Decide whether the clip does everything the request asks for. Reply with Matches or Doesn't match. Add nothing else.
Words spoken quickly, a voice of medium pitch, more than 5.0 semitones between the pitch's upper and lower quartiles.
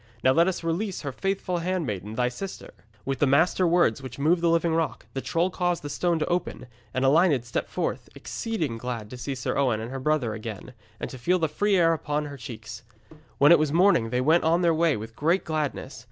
Matches